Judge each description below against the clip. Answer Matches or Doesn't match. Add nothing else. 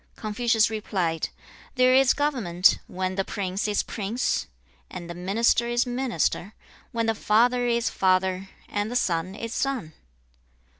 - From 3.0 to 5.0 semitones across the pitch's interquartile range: Matches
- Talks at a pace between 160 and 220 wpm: Doesn't match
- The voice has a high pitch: Matches